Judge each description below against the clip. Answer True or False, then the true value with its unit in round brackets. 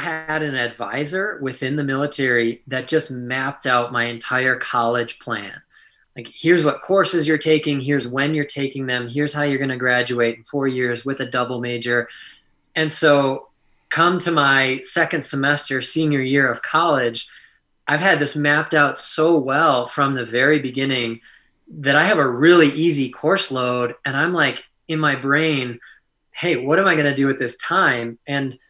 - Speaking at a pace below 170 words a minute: False (180 wpm)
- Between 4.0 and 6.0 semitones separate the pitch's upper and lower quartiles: False (3.3 semitones)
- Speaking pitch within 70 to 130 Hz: False (140 Hz)